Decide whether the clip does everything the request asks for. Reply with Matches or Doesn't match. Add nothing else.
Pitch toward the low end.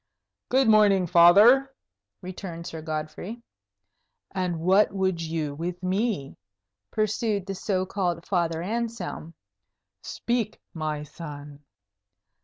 Doesn't match